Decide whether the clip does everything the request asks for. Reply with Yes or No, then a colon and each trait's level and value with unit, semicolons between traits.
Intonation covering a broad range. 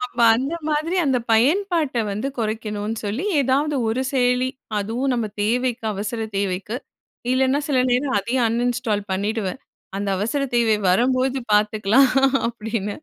No: average, 3.7 semitones